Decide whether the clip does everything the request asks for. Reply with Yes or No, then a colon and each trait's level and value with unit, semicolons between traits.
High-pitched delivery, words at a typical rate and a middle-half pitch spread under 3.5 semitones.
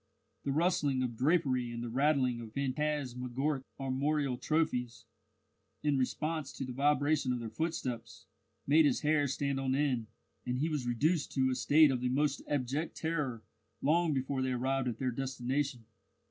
No: low, 135 Hz; average, 160 wpm; average, 2.9 semitones